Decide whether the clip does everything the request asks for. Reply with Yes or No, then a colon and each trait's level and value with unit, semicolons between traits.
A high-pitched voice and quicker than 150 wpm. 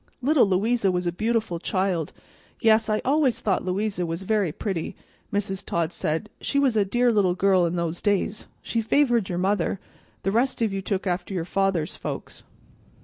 Yes: high, 195 Hz; average, 180 wpm